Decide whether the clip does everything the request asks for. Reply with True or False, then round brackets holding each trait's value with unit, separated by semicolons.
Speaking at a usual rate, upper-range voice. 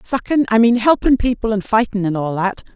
True (195 wpm; 220 Hz)